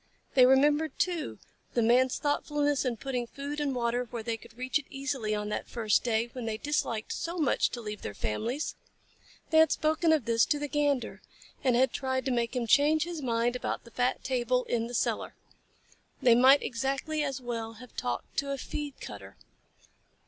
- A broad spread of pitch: No, average, 3.6 semitones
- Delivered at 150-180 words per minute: No, average, 190 wpm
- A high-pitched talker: Yes, very high, 255 Hz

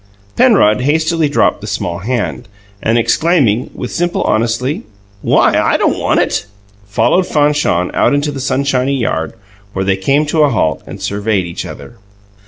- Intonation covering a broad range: Yes, wide, 6.2 semitones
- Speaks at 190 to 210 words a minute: No, average, 160 wpm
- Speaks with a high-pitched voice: No, low, 130 Hz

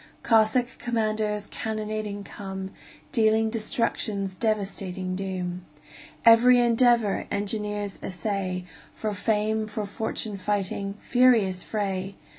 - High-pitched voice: Yes, high, 210 Hz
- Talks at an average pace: No, slow, 90 wpm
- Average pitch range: No, narrow, 2.2 semitones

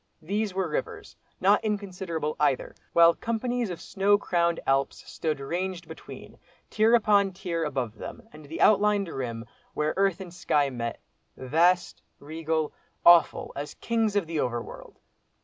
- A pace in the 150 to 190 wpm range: No, average, 140 wpm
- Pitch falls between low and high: Yes, medium, 170 Hz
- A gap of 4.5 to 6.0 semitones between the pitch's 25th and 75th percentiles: Yes, average, 5.2 semitones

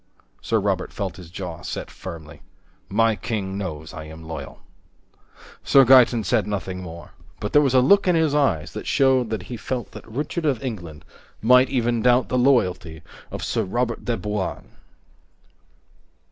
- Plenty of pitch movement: Yes, wide, 5.7 semitones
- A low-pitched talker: Yes, low, 110 Hz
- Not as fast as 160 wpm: No, average, 165 wpm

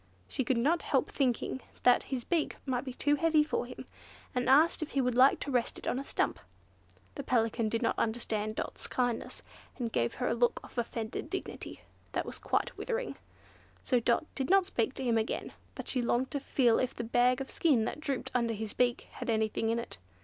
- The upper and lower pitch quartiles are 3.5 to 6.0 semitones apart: No, average, 2.8 semitones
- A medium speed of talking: No, fast, 215 wpm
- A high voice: Yes, high, 245 Hz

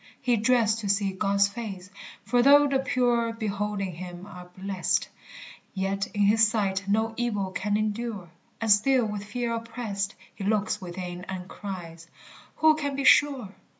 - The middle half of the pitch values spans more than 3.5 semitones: No, average, 3.2 semitones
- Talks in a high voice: Yes, high, 210 Hz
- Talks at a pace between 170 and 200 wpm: No, average, 155 wpm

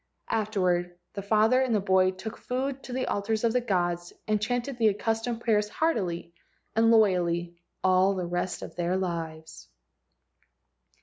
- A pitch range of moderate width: Yes, average, 4.3 semitones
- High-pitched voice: Yes, high, 200 Hz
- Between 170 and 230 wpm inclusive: No, average, 160 wpm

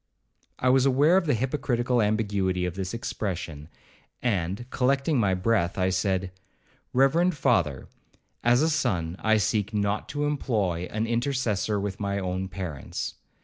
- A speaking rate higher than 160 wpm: No, average, 145 wpm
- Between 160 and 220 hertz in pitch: No, low, 105 Hz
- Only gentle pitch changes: No, average, 5.3 semitones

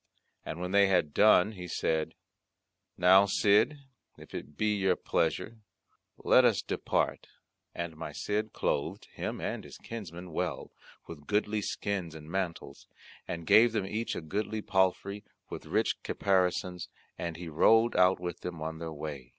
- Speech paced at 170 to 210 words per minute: No, average, 155 wpm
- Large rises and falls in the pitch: No, average, 3.8 semitones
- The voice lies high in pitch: No, very low, 90 Hz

